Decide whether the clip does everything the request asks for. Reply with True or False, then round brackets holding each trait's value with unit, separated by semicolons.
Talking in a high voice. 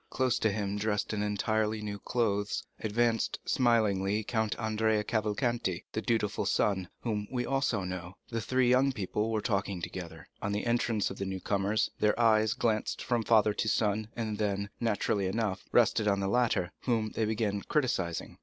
False (110 Hz)